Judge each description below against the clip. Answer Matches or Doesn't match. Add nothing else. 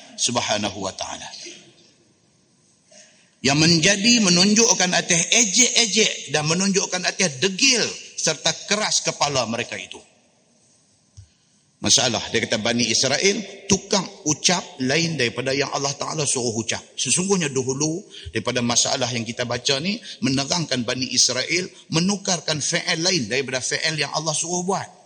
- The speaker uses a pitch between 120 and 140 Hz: Doesn't match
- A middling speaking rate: Matches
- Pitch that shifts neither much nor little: Doesn't match